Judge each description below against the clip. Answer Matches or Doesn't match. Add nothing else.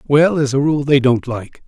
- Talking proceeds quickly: Matches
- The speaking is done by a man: Matches